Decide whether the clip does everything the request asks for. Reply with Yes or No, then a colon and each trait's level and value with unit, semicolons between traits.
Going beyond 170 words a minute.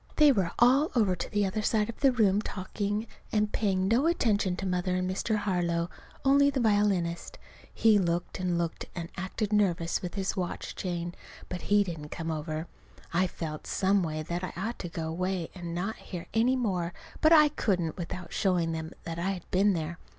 Yes: average, 195 wpm